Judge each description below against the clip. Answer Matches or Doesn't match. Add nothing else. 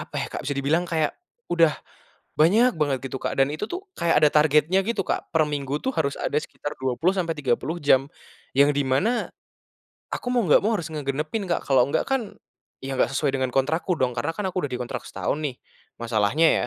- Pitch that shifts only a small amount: Doesn't match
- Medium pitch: Matches